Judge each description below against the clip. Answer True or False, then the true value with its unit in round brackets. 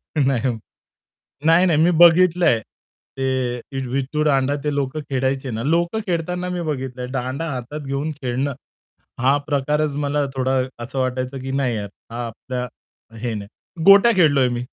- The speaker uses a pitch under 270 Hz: True (135 Hz)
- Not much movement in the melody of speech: False (3.4 semitones)